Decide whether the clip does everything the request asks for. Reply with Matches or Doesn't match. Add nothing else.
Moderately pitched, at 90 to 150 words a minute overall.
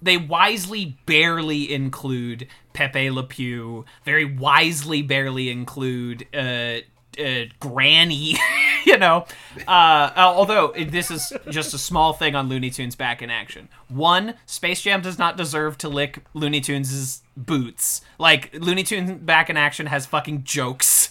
Matches